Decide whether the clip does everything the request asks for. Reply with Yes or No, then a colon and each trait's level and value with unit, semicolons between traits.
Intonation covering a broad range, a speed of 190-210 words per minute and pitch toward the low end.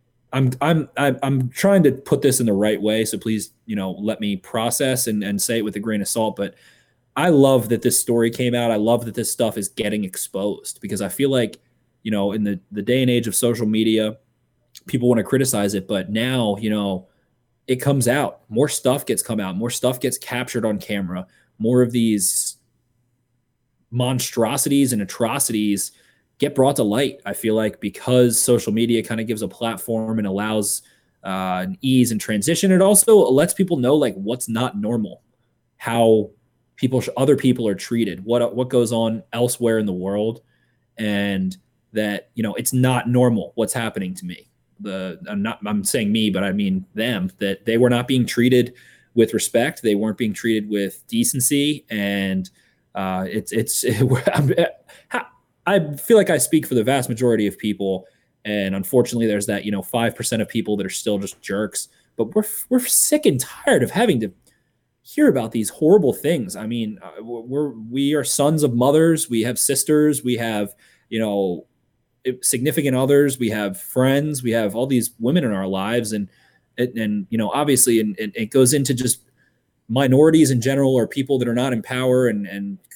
No: average, 3.6 semitones; average, 195 wpm; low, 115 Hz